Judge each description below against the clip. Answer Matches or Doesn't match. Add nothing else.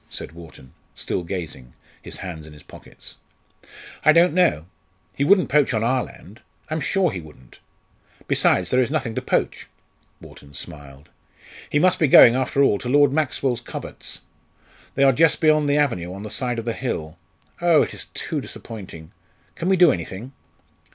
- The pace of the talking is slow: Doesn't match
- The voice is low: Matches